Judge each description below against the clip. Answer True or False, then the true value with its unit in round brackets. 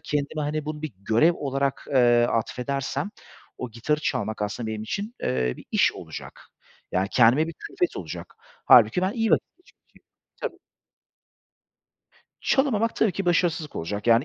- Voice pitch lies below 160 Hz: True (140 Hz)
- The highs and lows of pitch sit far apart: True (7.0 semitones)